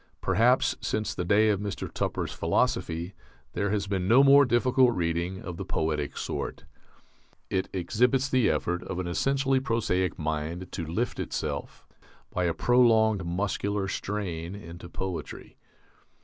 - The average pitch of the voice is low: Yes, very low, 95 Hz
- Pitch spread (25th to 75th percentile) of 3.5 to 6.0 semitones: Yes, average, 4.9 semitones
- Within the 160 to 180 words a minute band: No, average, 140 wpm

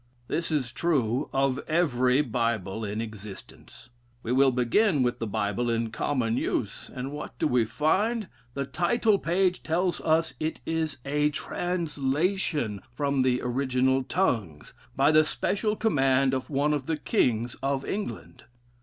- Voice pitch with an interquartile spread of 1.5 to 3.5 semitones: No, average, 4.8 semitones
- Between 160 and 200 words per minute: No, average, 145 wpm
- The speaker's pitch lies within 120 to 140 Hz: Yes, low, 135 Hz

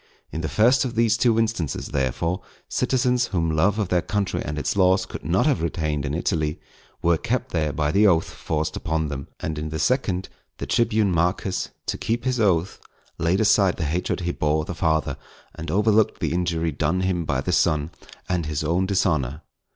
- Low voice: Yes, very low, 85 Hz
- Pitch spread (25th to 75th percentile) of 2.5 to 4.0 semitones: No, average, 4.6 semitones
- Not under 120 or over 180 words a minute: No, average, 195 wpm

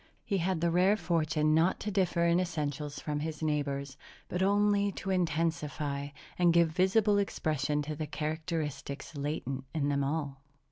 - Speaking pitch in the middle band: Yes, medium, 160 Hz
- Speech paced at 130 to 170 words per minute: Yes, average, 155 wpm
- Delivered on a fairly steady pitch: No, average, 3.5 semitones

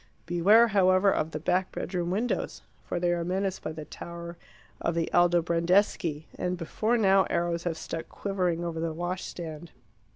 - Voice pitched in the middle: Yes, medium, 175 Hz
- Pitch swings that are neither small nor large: No, narrow, 2.0 semitones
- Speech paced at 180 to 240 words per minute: No, average, 160 wpm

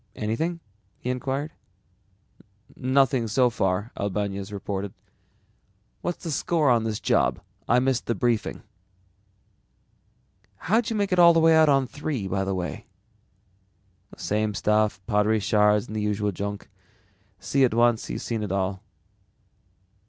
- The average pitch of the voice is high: No, low, 115 Hz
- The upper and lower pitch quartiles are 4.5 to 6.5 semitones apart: Yes, average, 4.8 semitones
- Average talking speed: No, slow, 130 wpm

